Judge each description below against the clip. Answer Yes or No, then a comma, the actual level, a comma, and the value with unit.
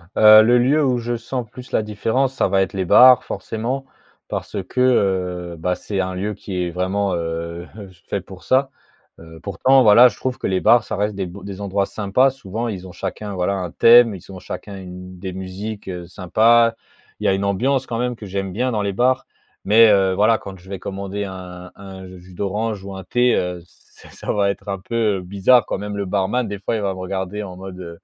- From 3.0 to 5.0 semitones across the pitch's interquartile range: Yes, average, 3.5 semitones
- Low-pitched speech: Yes, low, 100 Hz